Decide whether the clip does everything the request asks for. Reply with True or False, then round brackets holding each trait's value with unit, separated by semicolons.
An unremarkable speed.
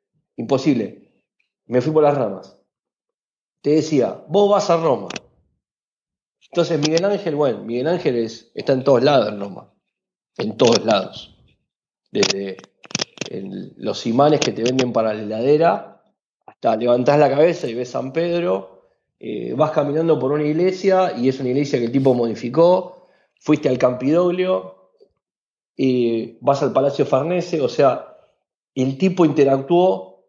True (145 wpm)